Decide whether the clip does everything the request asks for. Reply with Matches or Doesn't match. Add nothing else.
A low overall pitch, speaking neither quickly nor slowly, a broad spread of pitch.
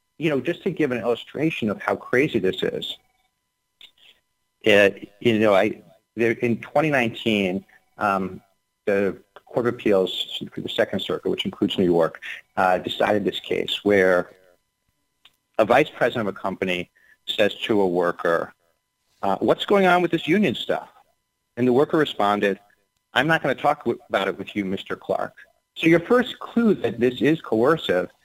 Matches